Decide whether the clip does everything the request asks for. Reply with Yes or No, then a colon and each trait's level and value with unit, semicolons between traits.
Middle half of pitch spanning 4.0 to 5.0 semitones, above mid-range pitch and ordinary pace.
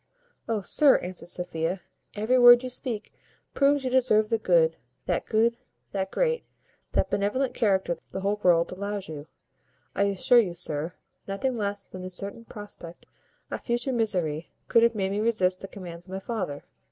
Yes: average, 4.5 semitones; high, 200 Hz; average, 165 wpm